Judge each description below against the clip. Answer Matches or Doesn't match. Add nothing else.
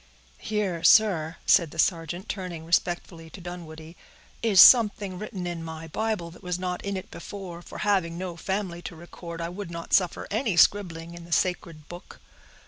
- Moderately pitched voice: Matches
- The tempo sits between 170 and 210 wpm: Matches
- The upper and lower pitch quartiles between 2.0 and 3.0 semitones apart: Matches